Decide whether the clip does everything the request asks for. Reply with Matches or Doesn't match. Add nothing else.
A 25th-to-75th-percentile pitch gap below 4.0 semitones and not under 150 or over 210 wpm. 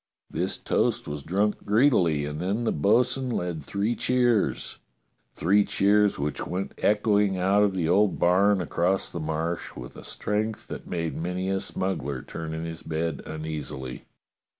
Doesn't match